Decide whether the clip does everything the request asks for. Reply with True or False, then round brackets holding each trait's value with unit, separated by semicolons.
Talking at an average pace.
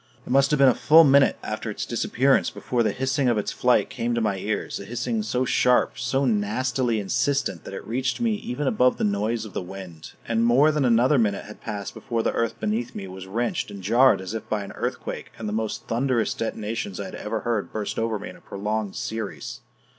False (225 wpm)